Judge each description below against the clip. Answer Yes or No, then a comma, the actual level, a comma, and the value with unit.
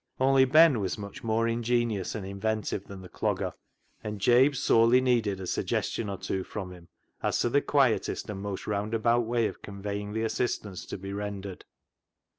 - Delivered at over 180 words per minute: No, average, 175 wpm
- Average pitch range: Yes, average, 3.2 semitones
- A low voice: Yes, low, 110 Hz